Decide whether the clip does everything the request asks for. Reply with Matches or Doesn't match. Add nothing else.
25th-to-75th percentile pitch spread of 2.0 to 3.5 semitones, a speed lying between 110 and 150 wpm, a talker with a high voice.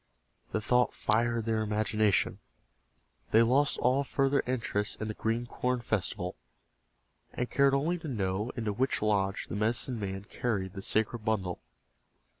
Doesn't match